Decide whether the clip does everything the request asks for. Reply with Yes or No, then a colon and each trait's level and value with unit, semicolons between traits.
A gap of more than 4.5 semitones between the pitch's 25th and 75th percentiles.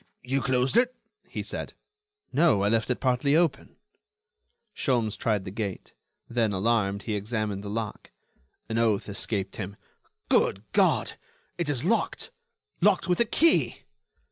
Yes: average, 5.1 semitones